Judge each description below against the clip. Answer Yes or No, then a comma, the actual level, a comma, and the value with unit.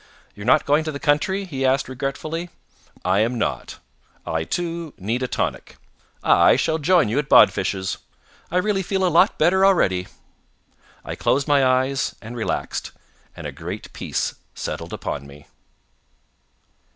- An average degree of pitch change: No, wide, 6.7 semitones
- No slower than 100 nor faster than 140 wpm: No, average, 150 wpm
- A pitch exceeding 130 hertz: Yes, medium, 140 Hz